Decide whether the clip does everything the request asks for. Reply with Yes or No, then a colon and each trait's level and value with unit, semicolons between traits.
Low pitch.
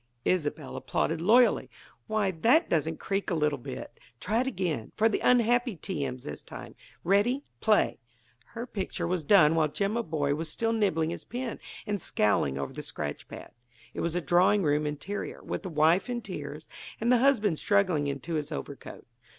No: medium, 180 Hz